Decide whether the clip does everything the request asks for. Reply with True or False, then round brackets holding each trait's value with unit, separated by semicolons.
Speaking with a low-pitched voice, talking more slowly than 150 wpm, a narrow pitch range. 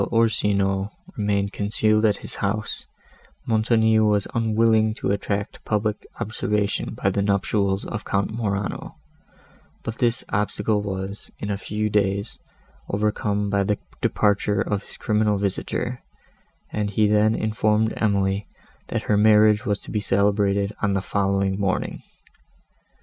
True (105 Hz; 135 wpm; 1.4 semitones)